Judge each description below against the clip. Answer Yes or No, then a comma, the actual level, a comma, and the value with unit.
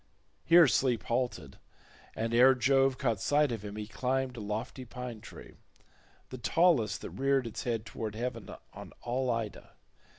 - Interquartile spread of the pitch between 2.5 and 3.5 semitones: Yes, average, 3.0 semitones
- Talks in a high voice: No, low, 120 Hz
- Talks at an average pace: Yes, average, 155 wpm